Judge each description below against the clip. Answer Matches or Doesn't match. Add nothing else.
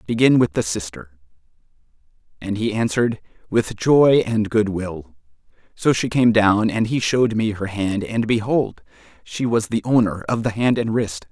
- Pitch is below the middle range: Matches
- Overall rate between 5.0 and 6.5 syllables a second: Doesn't match